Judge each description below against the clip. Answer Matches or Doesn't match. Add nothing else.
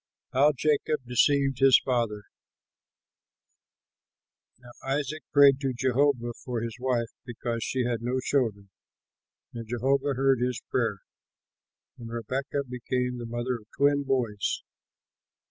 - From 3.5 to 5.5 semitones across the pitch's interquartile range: Doesn't match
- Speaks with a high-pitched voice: Doesn't match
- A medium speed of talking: Doesn't match